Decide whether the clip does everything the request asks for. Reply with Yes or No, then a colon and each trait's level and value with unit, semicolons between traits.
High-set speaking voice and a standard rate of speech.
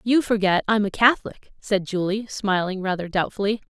Yes: high, 205 Hz; average, 160 wpm